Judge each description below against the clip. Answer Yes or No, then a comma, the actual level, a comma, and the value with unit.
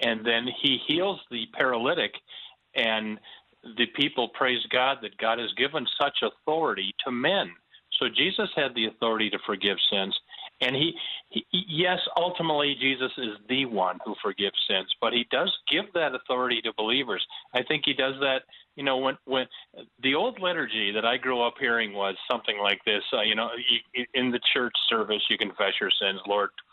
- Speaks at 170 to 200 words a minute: Yes, average, 180 wpm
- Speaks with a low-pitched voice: Yes, low, 125 Hz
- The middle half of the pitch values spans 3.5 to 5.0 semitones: Yes, average, 3.8 semitones